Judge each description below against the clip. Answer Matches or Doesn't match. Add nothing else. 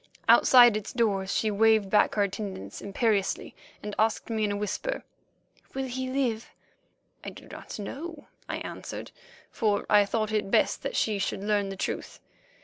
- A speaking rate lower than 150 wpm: Doesn't match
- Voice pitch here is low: Doesn't match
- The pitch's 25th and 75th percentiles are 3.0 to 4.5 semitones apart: Doesn't match